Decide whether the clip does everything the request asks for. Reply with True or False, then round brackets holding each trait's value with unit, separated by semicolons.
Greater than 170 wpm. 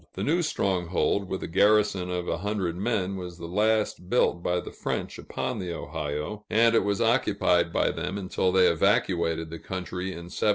True (190 wpm)